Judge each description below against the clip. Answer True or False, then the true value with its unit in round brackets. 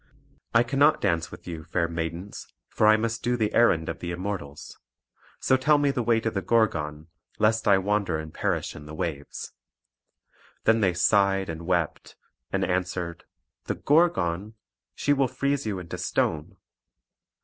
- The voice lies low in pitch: True (95 Hz)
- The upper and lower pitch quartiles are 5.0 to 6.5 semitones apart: True (5.5 semitones)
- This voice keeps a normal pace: True (160 wpm)